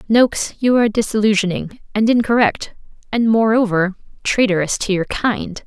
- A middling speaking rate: No, slow, 125 wpm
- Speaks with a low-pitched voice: No, high, 215 Hz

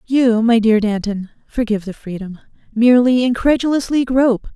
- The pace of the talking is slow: Yes, slow, 130 wpm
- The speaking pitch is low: No, high, 230 Hz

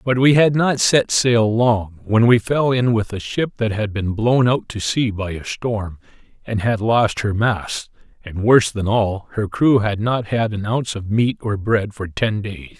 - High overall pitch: No, low, 110 Hz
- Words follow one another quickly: Yes, fast, 220 wpm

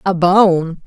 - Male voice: No, female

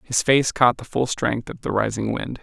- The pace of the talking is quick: Yes, fast, 250 wpm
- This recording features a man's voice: Yes, male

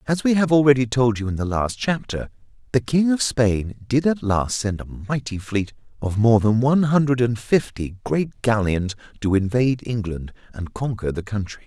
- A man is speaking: Yes, male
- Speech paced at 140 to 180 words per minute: No, average, 190 wpm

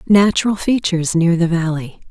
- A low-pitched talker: No, medium, 180 Hz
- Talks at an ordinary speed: Yes, average, 145 wpm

